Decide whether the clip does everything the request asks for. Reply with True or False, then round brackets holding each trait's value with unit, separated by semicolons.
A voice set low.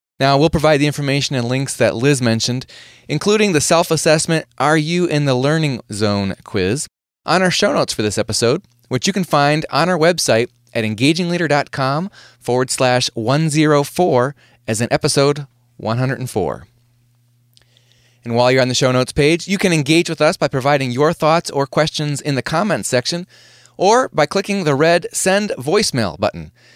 False (145 Hz)